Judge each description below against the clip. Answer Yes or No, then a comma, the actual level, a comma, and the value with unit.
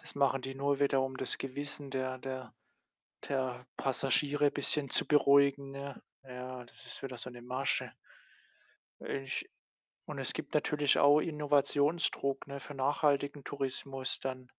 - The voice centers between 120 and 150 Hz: Yes, low, 135 Hz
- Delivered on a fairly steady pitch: Yes, narrow, 1.5 semitones